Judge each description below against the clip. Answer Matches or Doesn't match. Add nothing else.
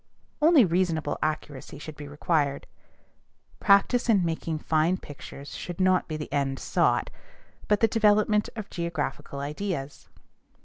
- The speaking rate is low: Matches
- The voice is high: Doesn't match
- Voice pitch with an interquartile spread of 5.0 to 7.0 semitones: Matches